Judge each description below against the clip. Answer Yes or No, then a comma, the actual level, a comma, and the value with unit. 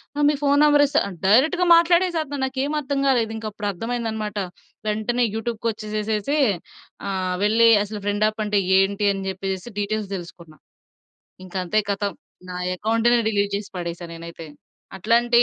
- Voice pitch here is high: Yes, high, 215 Hz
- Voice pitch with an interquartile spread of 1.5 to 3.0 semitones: No, average, 3.6 semitones